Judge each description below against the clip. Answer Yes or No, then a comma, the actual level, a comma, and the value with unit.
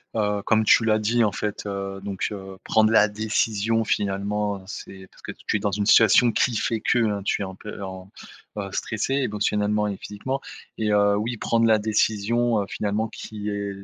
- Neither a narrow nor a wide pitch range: No, narrow, 1.6 semitones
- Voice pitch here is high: No, low, 105 Hz